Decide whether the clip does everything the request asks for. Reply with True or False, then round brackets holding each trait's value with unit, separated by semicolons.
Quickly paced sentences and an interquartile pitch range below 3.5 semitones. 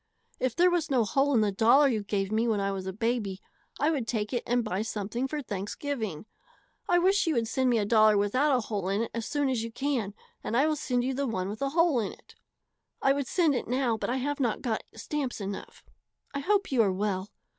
False (245 wpm; 4.9 semitones)